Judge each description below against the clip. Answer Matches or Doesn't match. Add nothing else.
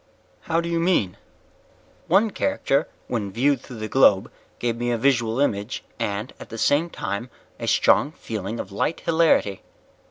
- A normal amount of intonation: Doesn't match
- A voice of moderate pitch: Doesn't match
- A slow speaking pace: Doesn't match